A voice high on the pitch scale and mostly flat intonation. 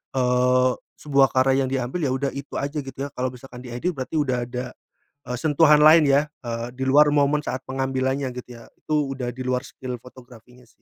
No: low, 130 Hz; narrow, 2.0 semitones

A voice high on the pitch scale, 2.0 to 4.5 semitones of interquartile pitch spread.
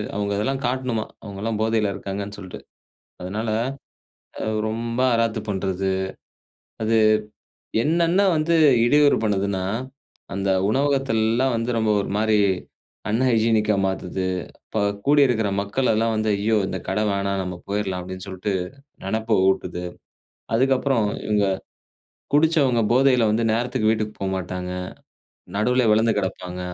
No: low, 110 Hz; average, 3.5 semitones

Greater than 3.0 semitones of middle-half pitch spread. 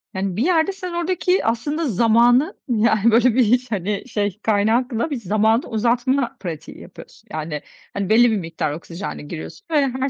Yes: average, 4.4 semitones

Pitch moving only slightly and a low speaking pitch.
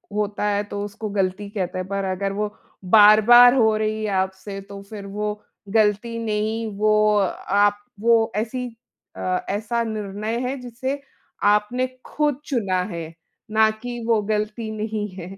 No: narrow, 1.9 semitones; high, 210 Hz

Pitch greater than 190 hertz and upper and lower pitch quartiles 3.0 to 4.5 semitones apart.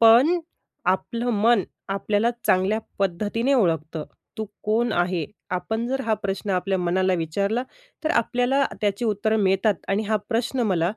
Yes: high, 210 Hz; average, 3.7 semitones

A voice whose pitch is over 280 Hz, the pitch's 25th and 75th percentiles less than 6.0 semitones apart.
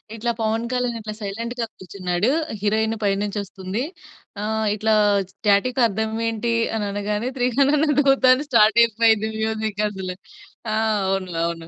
No: high, 220 Hz; narrow, 2.6 semitones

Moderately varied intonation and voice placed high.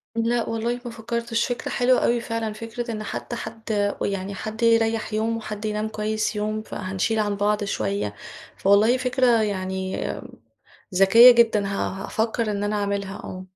No: narrow, 2.3 semitones; high, 215 Hz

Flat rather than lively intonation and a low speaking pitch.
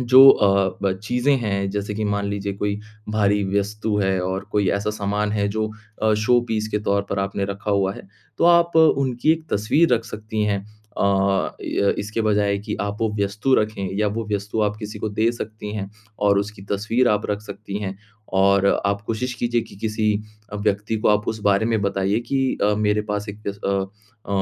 Yes: narrow, 1.5 semitones; low, 105 Hz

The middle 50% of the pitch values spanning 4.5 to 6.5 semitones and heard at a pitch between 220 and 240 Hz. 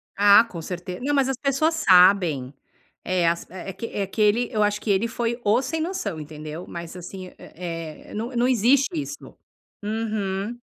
No: average, 5.1 semitones; high, 205 Hz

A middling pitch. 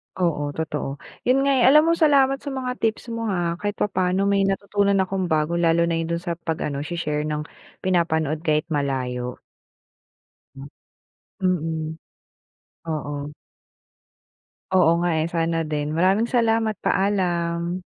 Yes: medium, 170 Hz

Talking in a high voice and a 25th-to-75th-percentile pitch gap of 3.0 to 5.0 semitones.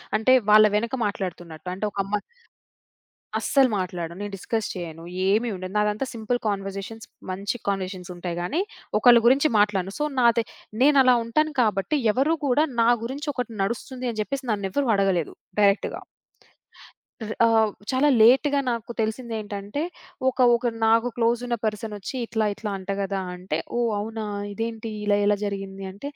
Yes: high, 215 Hz; average, 3.5 semitones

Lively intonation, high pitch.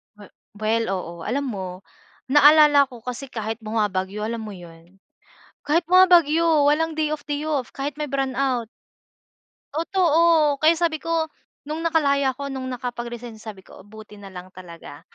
Yes: wide, 6.2 semitones; very high, 265 Hz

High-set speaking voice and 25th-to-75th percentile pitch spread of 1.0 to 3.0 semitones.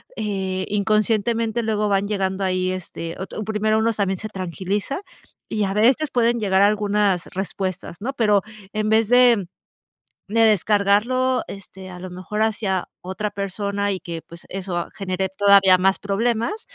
Yes: high, 200 Hz; narrow, 2.4 semitones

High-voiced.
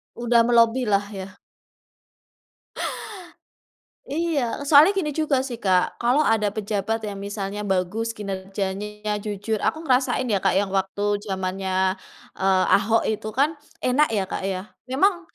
Yes: high, 210 Hz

